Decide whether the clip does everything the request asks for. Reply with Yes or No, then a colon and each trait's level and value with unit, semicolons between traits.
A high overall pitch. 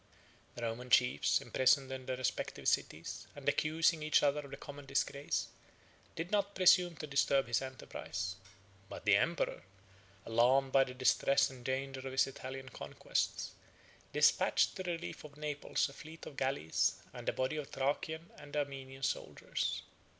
No: low, 135 Hz